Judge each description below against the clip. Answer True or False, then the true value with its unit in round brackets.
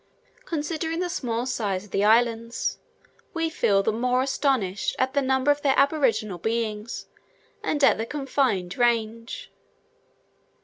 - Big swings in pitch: False (4.3 semitones)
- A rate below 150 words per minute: True (135 wpm)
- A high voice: True (240 Hz)